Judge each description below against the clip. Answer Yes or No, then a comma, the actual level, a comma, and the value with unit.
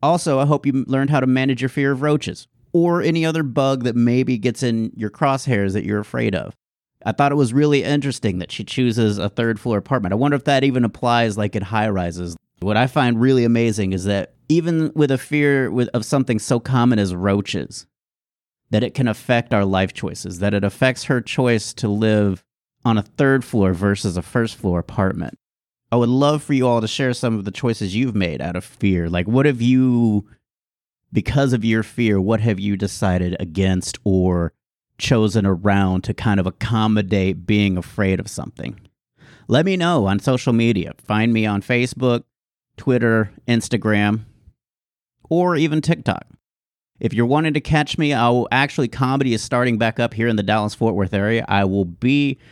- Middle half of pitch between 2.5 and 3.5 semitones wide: No, average, 4.5 semitones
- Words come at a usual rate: Yes, average, 195 wpm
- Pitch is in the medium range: No, low, 115 Hz